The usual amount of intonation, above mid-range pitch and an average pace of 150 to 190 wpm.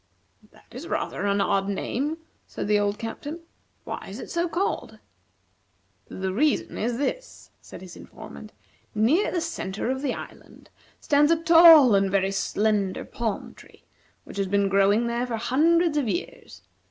No: wide, 7.5 semitones; high, 235 Hz; average, 160 wpm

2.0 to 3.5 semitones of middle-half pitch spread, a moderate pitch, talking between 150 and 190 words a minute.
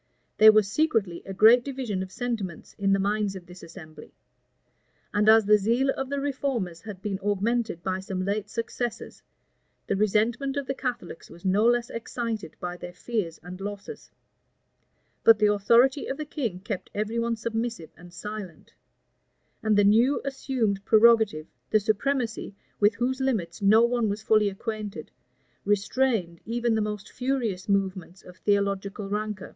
No: average, 3.2 semitones; high, 210 Hz; average, 160 wpm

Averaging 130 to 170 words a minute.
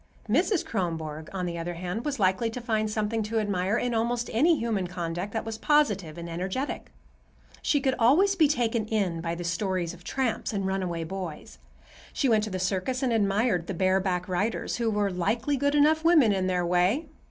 No: average, 195 wpm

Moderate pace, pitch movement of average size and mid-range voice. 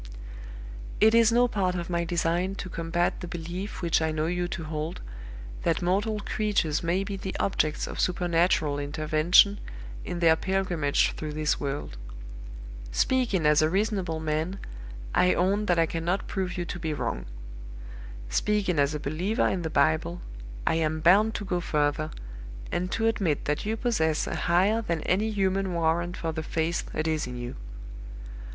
Yes: average, 170 wpm; average, 3.6 semitones; medium, 175 Hz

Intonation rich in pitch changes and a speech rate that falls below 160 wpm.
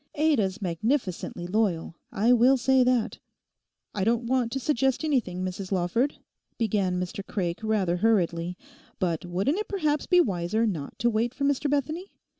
Yes: wide, 6.5 semitones; average, 150 wpm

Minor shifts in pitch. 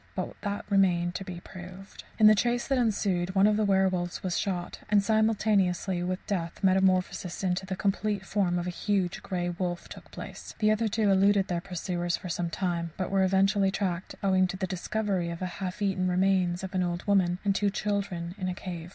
Yes: narrow, 2.1 semitones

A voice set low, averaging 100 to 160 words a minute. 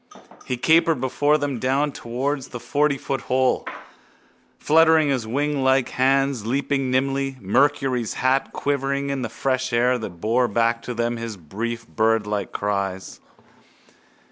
Yes: low, 130 Hz; slow, 135 wpm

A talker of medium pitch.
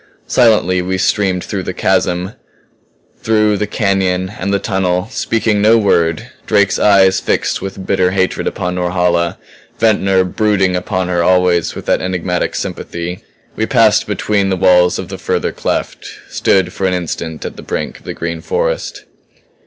No: very low, 95 Hz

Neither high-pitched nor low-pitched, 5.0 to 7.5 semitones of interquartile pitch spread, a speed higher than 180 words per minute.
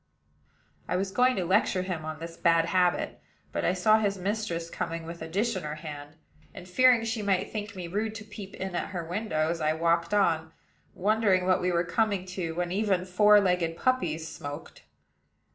No: medium, 180 Hz; average, 3.7 semitones; average, 195 wpm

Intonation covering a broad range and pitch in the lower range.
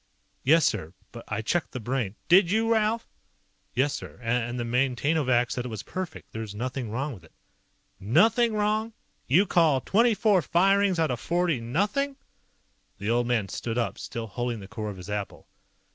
Yes: wide, 8.5 semitones; low, 130 Hz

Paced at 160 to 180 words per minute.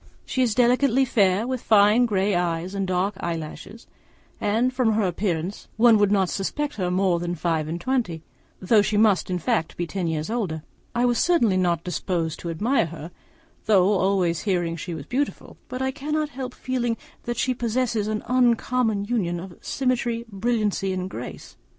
Yes: average, 175 wpm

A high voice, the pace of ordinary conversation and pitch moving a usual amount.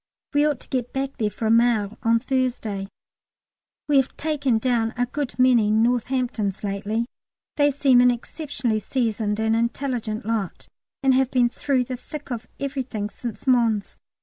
Yes: high, 245 Hz; average, 160 wpm; average, 3.1 semitones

